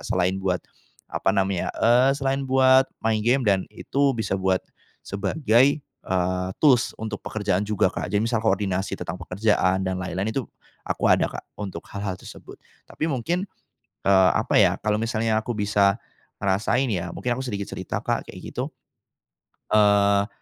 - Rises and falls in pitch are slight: No, average, 4.2 semitones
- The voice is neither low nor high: No, low, 105 Hz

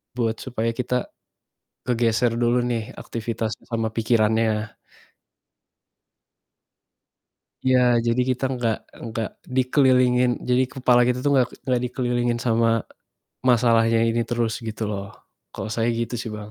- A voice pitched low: Yes, low, 120 Hz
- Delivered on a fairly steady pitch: Yes, narrow, 1.7 semitones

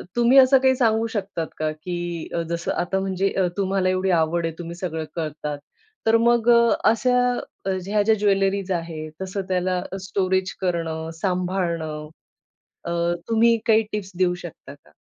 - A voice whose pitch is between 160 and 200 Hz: Yes, medium, 185 Hz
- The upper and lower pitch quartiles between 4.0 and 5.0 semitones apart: Yes, average, 4.4 semitones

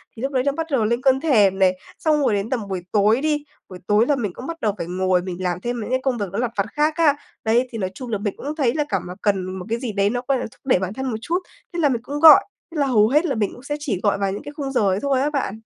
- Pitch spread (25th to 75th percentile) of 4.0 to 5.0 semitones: No, wide, 5.6 semitones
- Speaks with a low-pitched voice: No, high, 240 Hz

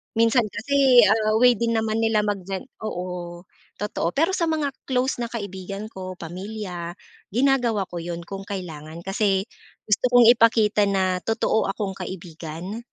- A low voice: No, high, 205 Hz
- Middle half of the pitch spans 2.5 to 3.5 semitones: No, average, 3.9 semitones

